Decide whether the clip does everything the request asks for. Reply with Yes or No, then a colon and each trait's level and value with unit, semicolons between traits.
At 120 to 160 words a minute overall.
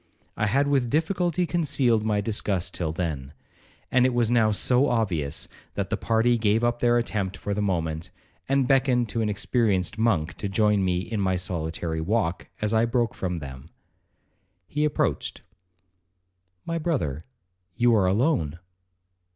Yes: average, 155 wpm